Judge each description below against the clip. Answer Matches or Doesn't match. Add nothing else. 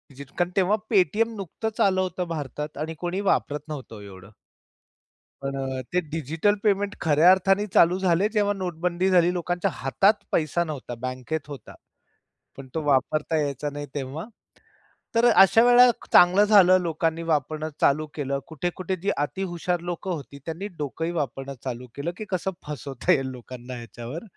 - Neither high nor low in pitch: Matches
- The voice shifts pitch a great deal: Doesn't match